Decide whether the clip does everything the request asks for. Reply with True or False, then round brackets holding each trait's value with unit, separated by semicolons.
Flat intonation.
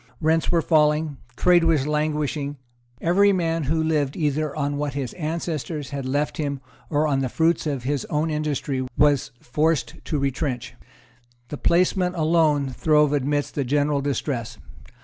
True (2.2 semitones)